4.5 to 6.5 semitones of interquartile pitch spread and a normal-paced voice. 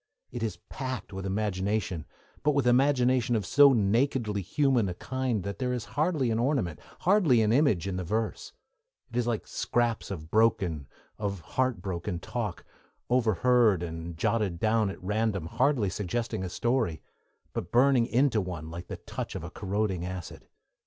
Yes: average, 5.1 semitones; average, 165 wpm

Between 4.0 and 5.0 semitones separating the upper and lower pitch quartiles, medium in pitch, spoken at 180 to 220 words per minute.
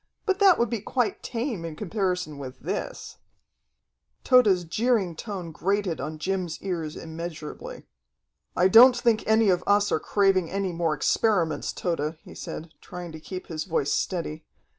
No: average, 4.7 semitones; medium, 180 Hz; average, 155 wpm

